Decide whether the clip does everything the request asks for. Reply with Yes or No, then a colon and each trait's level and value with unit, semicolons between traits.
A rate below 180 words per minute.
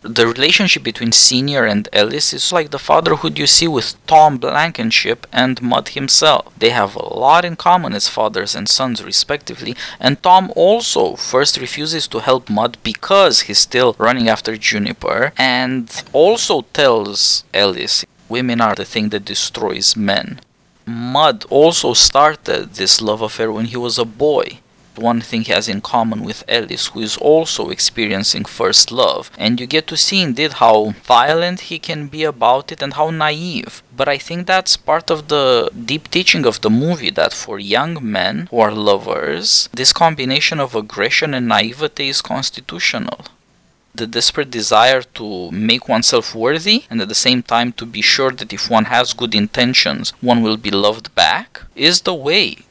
Yes: average, 170 wpm